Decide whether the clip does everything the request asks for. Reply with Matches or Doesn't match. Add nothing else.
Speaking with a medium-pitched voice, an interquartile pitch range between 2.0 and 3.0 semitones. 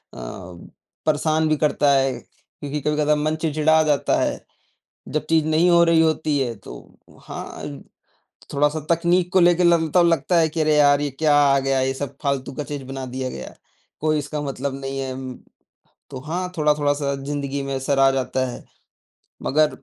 Matches